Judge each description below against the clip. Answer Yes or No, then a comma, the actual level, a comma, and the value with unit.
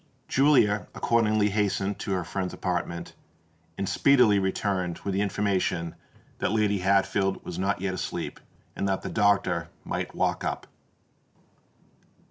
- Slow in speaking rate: Yes, slow, 130 wpm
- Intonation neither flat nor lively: No, narrow, 1.9 semitones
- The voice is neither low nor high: No, low, 100 Hz